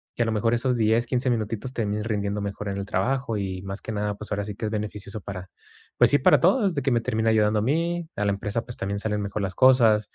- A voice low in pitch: Yes, low, 110 Hz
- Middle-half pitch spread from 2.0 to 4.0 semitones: Yes, average, 2.9 semitones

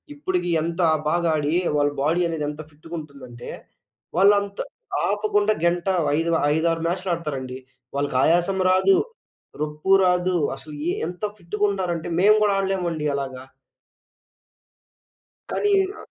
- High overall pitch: No, medium, 170 Hz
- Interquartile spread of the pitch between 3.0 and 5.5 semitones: Yes, average, 4.1 semitones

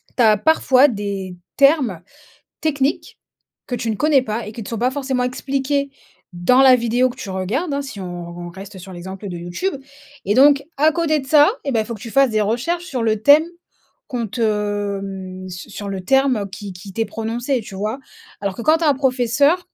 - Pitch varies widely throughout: Yes, wide, 5.8 semitones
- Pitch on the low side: No, high, 235 Hz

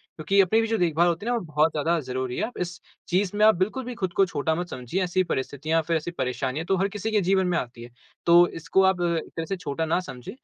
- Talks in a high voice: No, medium, 175 Hz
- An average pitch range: Yes, average, 3.7 semitones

